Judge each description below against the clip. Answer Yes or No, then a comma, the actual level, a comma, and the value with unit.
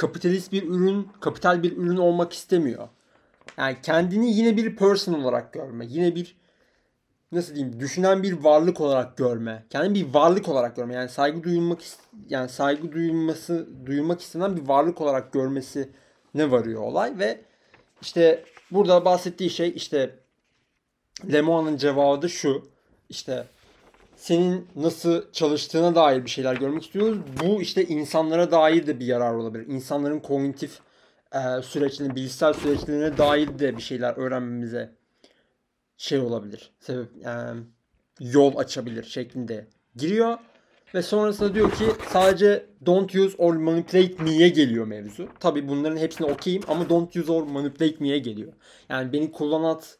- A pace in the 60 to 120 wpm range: No, average, 135 wpm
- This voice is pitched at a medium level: Yes, medium, 155 Hz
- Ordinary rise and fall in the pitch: Yes, average, 4.5 semitones